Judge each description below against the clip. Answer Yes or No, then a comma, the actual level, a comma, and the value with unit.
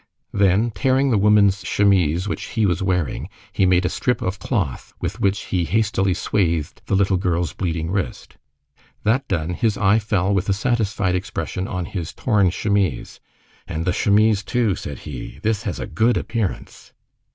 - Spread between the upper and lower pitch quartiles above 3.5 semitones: No, average, 2.9 semitones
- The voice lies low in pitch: Yes, very low, 95 Hz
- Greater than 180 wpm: No, average, 170 wpm